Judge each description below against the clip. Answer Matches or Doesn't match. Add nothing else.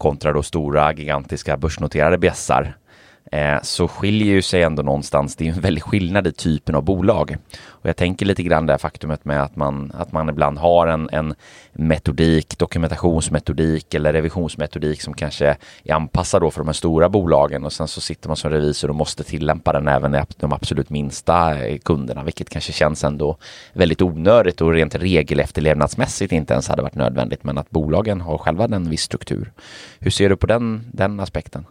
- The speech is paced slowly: Doesn't match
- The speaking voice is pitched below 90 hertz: Matches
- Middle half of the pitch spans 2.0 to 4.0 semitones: Matches